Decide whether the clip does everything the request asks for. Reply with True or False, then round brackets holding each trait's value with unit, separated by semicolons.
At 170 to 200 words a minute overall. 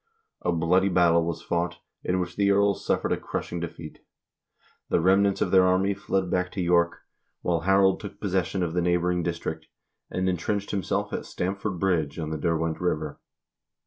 True (175 wpm)